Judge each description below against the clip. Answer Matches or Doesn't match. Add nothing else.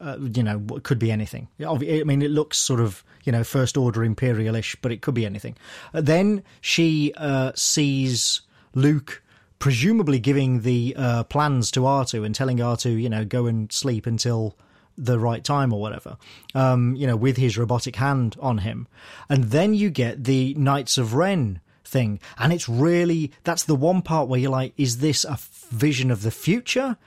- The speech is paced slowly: Doesn't match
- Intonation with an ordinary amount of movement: Matches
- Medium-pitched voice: Doesn't match